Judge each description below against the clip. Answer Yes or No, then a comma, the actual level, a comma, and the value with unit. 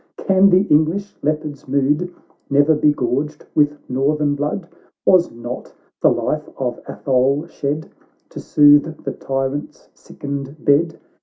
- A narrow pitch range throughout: Yes, narrow, 2.1 semitones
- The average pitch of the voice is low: No, medium, 145 Hz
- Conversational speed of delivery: No, slow, 130 wpm